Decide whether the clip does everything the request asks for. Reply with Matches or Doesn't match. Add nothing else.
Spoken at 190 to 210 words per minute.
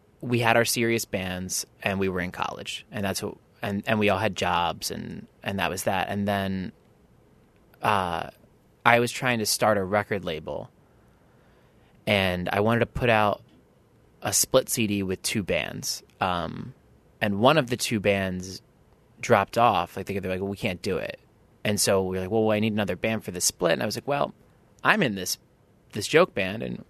Matches